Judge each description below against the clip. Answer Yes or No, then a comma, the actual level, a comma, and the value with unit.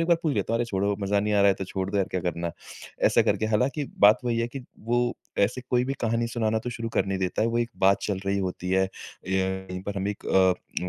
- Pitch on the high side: No, low, 100 Hz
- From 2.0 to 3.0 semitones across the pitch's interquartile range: No, average, 3.5 semitones